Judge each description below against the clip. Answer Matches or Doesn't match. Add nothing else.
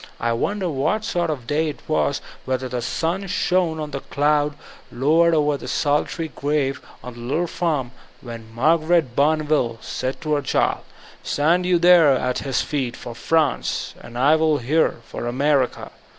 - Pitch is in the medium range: Matches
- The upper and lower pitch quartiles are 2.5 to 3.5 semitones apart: Doesn't match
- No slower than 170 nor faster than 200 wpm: Matches